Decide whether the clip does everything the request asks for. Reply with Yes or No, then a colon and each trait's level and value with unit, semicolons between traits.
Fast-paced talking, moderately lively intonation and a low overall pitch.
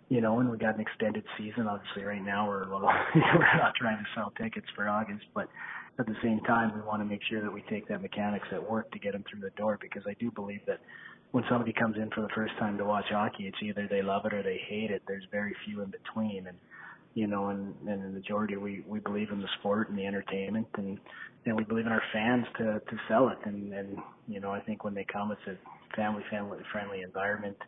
No: fast, 255 wpm; narrow, 1.4 semitones; low, 105 Hz